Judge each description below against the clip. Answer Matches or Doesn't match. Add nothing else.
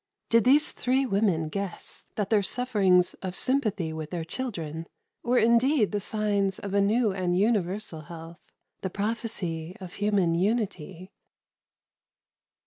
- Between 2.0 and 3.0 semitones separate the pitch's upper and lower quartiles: Doesn't match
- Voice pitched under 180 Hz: Doesn't match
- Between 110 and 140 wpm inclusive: Matches